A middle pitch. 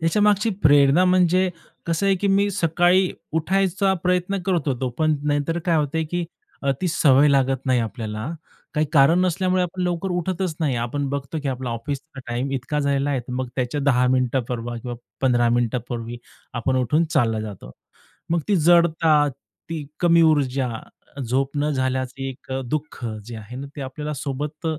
Yes: medium, 145 Hz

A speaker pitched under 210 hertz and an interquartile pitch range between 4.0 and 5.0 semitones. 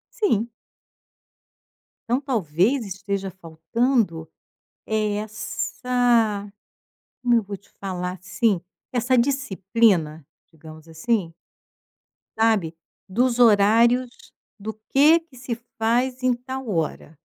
No: high, 220 Hz; average, 4.7 semitones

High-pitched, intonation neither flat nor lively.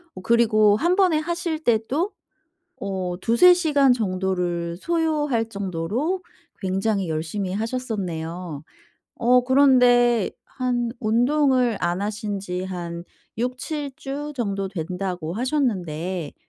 No: high, 220 Hz; wide, 6.2 semitones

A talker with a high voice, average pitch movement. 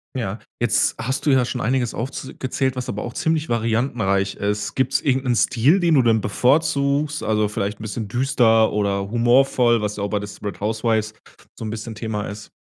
No: low, 115 Hz; average, 3.8 semitones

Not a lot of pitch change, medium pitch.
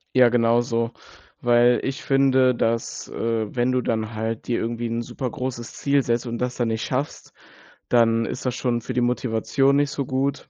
No: narrow, 1.9 semitones; low, 120 Hz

